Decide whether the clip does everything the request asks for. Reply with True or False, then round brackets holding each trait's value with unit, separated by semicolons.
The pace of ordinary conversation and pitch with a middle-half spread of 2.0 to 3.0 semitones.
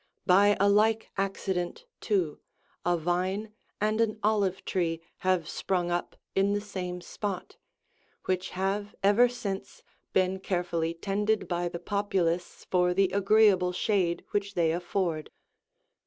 False (130 wpm; 2.5 semitones)